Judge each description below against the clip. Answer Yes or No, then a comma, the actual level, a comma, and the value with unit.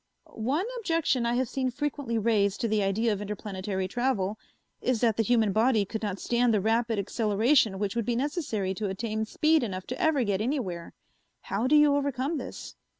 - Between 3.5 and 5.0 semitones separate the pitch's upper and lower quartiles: Yes, average, 4.1 semitones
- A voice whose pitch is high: Yes, high, 230 Hz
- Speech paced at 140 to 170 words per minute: No, average, 190 wpm